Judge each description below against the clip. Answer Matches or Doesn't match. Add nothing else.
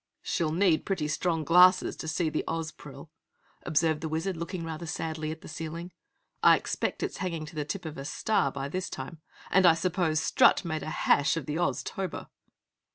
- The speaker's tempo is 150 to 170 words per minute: Doesn't match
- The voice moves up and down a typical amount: Doesn't match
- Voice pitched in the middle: Matches